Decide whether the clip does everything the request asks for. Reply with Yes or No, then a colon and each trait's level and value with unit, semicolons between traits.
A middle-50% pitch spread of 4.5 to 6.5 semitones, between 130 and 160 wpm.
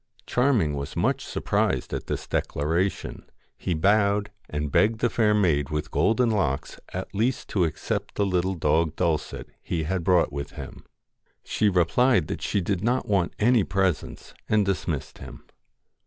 Yes: average, 4.8 semitones; average, 155 wpm